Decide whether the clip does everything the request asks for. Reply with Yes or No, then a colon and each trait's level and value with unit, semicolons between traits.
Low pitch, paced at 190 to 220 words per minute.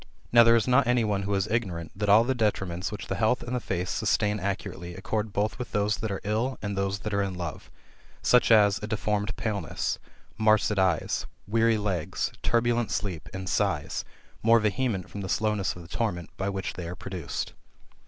Yes: low, 105 Hz; average, 200 wpm